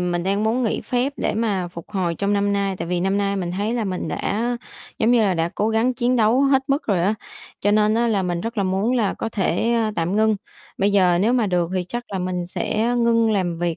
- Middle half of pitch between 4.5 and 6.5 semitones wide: No, average, 3.9 semitones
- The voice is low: No, high, 205 Hz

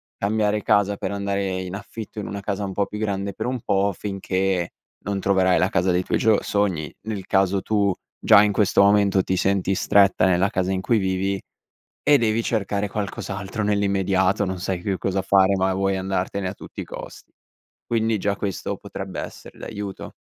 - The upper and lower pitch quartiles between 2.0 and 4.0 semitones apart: No, narrow, 1.4 semitones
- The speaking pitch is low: Yes, low, 100 Hz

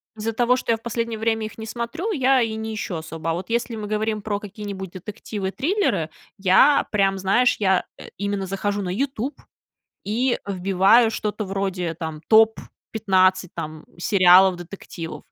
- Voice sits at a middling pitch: No, high, 205 Hz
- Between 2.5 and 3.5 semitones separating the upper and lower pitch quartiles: Yes, average, 3.2 semitones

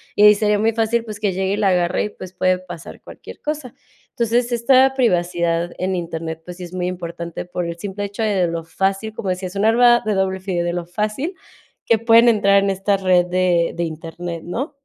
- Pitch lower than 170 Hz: No, high, 190 Hz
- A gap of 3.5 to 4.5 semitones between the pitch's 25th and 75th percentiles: Yes, average, 3.8 semitones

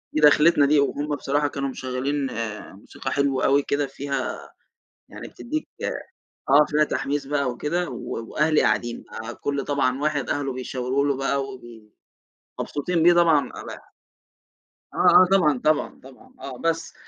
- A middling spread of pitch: No, narrow, 2.3 semitones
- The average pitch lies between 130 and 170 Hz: Yes, medium, 140 Hz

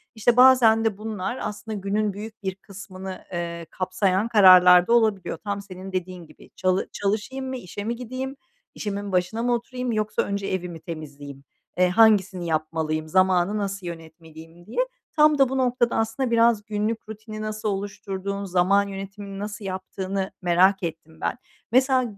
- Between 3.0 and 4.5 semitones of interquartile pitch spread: Yes, average, 3.4 semitones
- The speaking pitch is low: No, high, 200 Hz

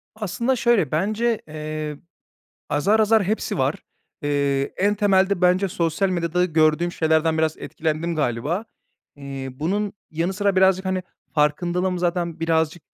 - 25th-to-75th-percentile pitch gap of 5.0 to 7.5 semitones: No, average, 3.9 semitones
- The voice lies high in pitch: No, medium, 175 Hz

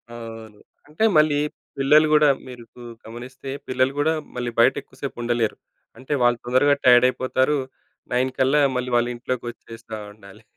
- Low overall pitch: Yes, low, 125 Hz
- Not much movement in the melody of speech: Yes, narrow, 2.3 semitones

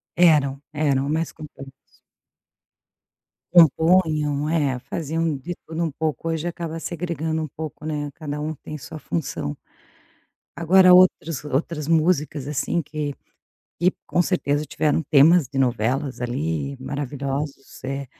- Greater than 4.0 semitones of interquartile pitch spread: No, average, 2.8 semitones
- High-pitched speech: No, medium, 150 Hz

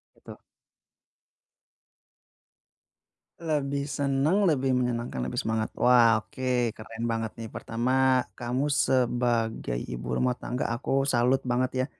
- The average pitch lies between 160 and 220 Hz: No, low, 125 Hz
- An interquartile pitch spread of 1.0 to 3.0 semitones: Yes, average, 2.7 semitones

